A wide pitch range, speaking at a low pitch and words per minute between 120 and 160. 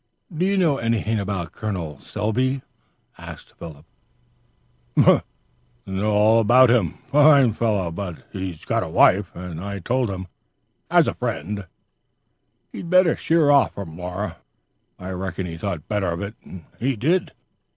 Yes: wide, 5.8 semitones; low, 100 Hz; average, 140 wpm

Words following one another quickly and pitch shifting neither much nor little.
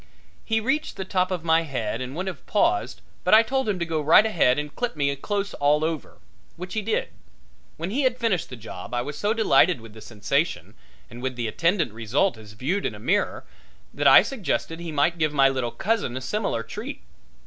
No: fast, 215 wpm; wide, 8.0 semitones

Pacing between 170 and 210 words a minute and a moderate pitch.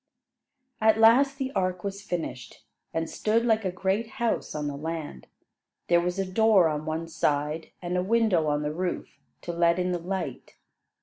Yes: average, 180 wpm; medium, 180 Hz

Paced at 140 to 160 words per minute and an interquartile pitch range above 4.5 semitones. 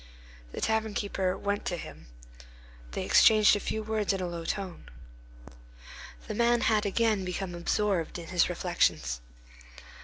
No: average, 145 wpm; average, 3.4 semitones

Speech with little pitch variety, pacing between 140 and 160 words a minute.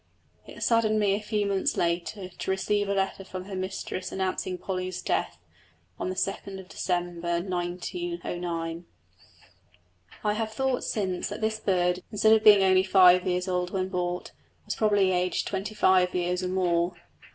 Yes: narrow, 2.3 semitones; average, 155 wpm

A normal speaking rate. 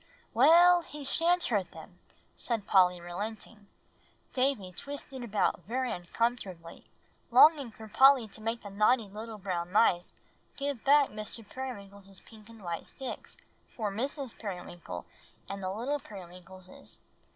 No: slow, 130 wpm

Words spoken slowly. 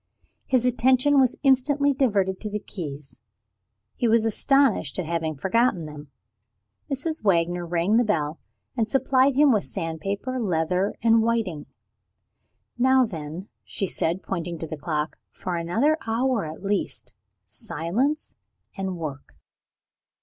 Yes: slow, 130 wpm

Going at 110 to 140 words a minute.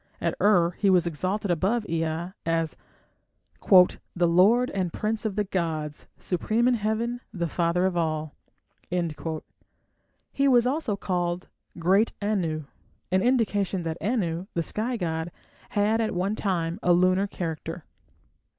Yes: slow, 135 wpm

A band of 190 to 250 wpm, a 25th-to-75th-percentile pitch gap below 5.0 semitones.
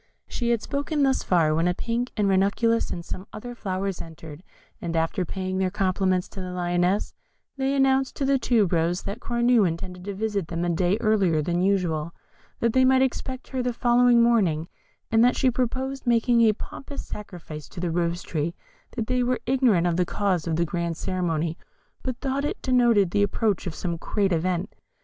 No: average, 195 wpm; wide, 5.6 semitones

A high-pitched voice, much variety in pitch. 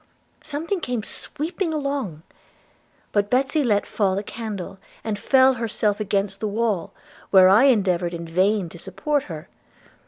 Yes: high, 210 Hz; wide, 5.7 semitones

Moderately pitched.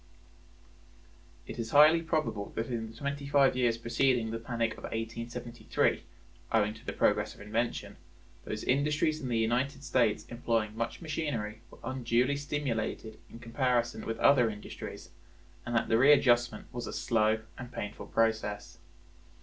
No: low, 115 Hz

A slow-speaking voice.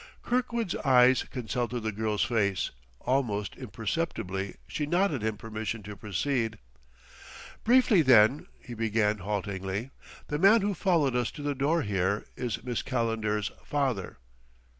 Yes: slow, 130 wpm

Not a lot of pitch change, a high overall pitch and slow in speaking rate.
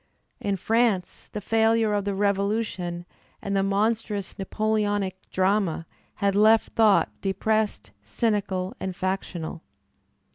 Yes: narrow, 2.2 semitones; high, 200 Hz; slow, 115 wpm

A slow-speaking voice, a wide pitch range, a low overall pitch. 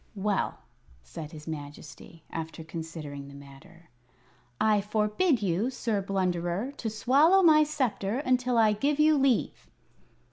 No: slow, 130 wpm; wide, 7.7 semitones; high, 205 Hz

